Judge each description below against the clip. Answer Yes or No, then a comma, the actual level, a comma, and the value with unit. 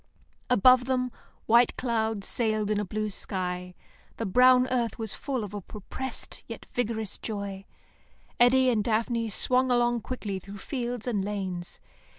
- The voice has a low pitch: No, high, 225 Hz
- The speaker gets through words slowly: No, average, 150 wpm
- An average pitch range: Yes, average, 3.4 semitones